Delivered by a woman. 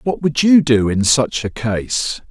No: male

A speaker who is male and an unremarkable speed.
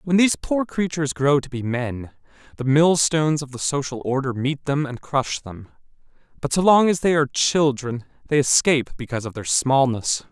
Yes: male; average, 185 wpm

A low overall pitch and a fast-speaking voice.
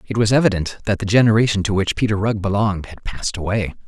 Yes: low, 105 Hz; fast, 215 wpm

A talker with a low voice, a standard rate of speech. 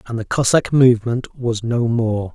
Yes: low, 120 Hz; average, 180 wpm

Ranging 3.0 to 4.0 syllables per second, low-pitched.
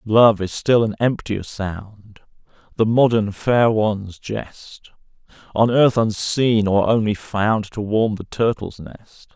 Yes: 3.7 syllables/s; low, 110 Hz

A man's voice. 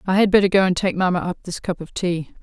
No: female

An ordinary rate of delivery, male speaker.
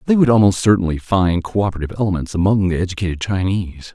Yes: average, 165 wpm; male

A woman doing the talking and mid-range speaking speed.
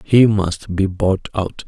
No: male; average, 180 wpm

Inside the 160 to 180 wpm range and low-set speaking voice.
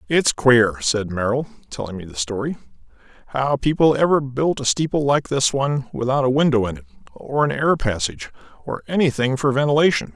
Yes: average, 175 wpm; low, 125 Hz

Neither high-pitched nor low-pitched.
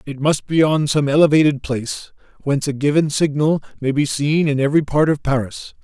Yes: medium, 145 Hz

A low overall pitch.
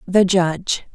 No: medium, 185 Hz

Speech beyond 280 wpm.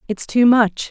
No: average, 200 wpm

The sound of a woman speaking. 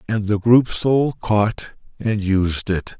No: male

